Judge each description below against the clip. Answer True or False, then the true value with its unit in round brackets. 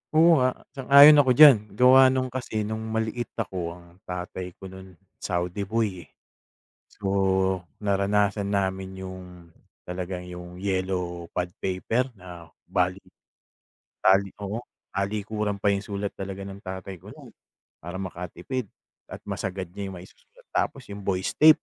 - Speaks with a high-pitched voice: False (95 Hz)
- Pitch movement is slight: False (3.0 semitones)